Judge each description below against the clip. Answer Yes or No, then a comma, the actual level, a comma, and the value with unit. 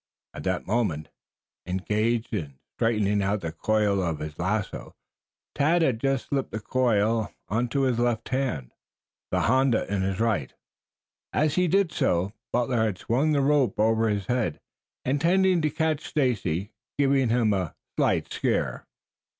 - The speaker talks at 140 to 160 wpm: Yes, average, 150 wpm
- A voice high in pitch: No, low, 115 Hz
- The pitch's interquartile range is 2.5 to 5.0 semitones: No, wide, 5.5 semitones